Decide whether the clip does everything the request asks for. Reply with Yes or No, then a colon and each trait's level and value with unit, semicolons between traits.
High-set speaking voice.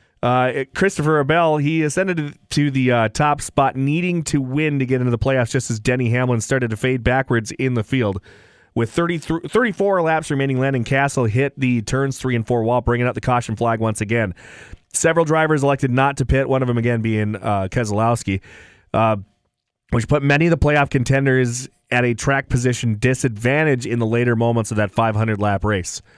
No: low, 125 Hz